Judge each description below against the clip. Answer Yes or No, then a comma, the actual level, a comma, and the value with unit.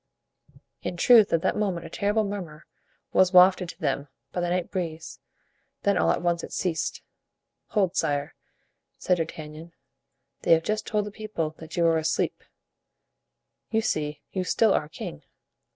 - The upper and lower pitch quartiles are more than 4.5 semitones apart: No, average, 3.9 semitones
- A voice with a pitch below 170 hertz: No, medium, 175 Hz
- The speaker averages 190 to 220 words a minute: No, average, 160 wpm